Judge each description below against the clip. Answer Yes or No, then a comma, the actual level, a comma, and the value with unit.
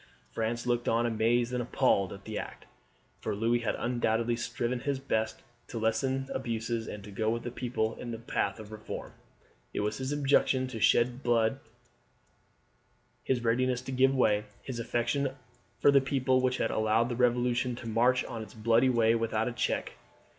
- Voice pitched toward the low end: Yes, low, 120 Hz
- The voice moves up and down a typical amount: No, narrow, 2.2 semitones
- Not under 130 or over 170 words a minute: No, average, 180 wpm